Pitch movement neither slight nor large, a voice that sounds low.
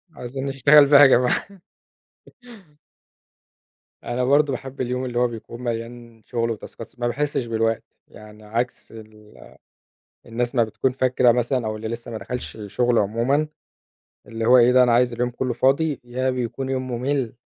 No: narrow, 2.0 semitones; low, 120 Hz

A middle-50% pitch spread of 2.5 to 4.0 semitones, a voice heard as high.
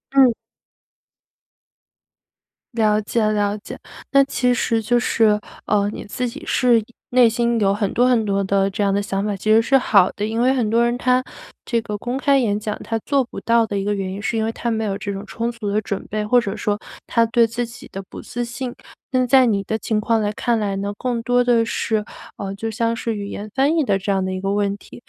Yes: average, 2.9 semitones; high, 225 Hz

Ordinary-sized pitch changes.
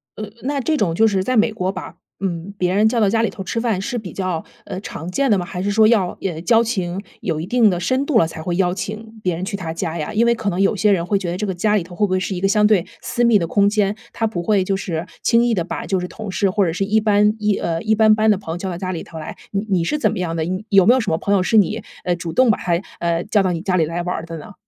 Yes: average, 3.5 semitones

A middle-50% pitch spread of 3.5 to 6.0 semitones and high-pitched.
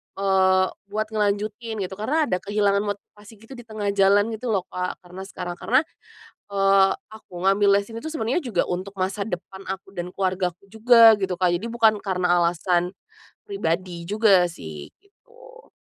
No: average, 3.0 semitones; high, 200 Hz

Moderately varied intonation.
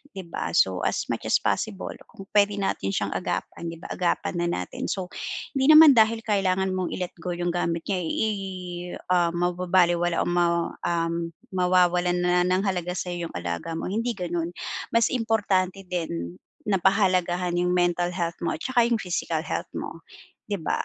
No: narrow, 2.1 semitones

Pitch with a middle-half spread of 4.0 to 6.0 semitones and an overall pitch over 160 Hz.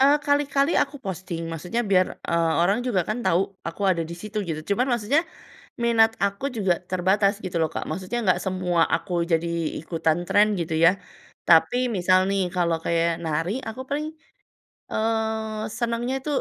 Yes: average, 4.8 semitones; high, 190 Hz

